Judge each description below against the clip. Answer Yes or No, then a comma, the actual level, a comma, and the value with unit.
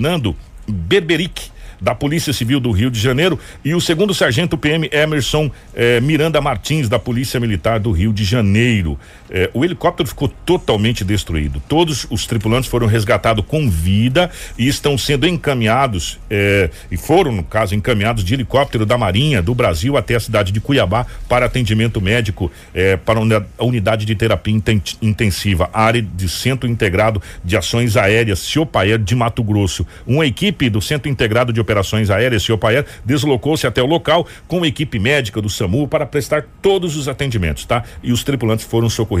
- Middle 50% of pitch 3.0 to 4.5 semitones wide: No, average, 5.2 semitones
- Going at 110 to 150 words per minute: No, average, 170 wpm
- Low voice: Yes, low, 115 Hz